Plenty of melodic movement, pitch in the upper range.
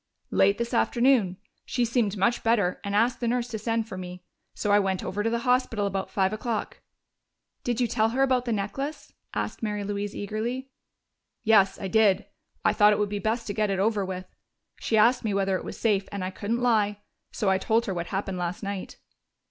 No: average, 3.1 semitones; high, 210 Hz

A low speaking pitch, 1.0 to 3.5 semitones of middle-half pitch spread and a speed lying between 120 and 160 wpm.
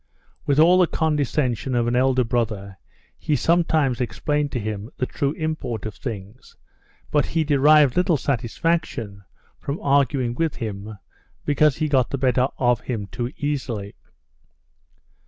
No: low, 130 Hz; average, 4.1 semitones; average, 140 wpm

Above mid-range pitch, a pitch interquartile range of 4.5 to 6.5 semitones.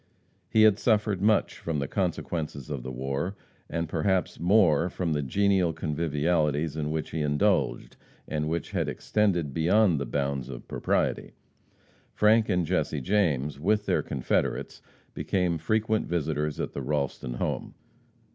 No: very low, 80 Hz; average, 4.8 semitones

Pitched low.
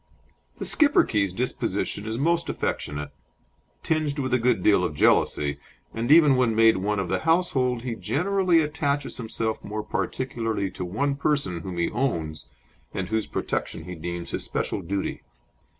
Yes: low, 115 Hz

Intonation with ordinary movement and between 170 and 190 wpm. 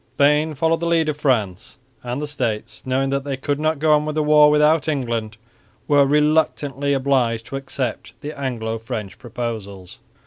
Yes: average, 4.3 semitones; average, 175 wpm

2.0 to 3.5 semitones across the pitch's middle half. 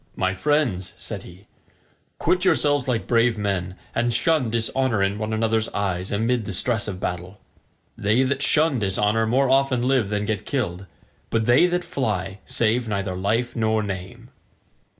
No: average, 4.3 semitones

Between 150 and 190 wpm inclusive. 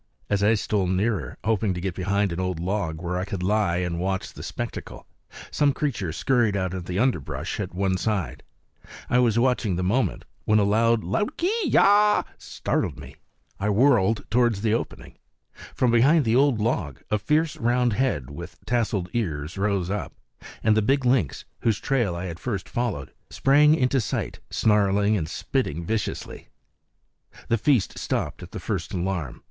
Yes: average, 170 wpm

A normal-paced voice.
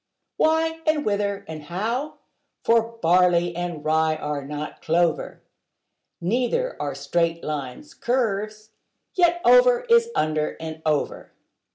No: slow, 120 wpm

